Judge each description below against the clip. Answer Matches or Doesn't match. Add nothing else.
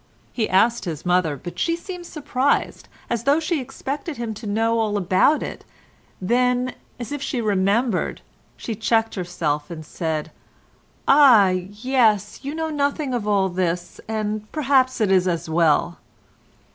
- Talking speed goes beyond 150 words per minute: Doesn't match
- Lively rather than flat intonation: Matches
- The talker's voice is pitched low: Doesn't match